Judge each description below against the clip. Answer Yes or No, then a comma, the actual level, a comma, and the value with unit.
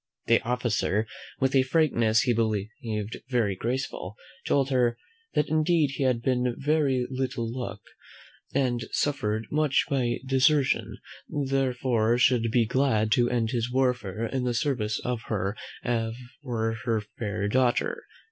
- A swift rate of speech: No, average, 140 wpm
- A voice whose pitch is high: No, low, 125 Hz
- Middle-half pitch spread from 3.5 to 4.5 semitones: No, average, 2.9 semitones